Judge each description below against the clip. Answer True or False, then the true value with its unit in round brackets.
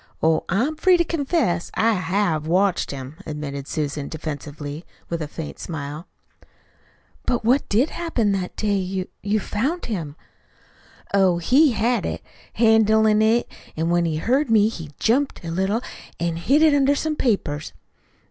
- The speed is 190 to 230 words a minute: False (155 wpm)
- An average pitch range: False (6.9 semitones)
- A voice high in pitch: True (200 Hz)